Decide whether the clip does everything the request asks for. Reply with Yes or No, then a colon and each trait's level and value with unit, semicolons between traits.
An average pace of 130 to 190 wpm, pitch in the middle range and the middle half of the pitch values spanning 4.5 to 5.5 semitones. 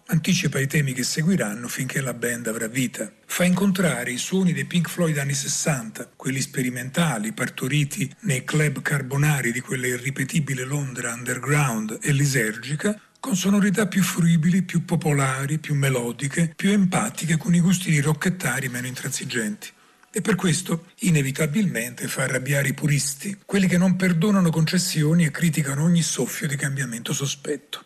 Yes: average, 150 wpm; medium, 150 Hz; average, 4.8 semitones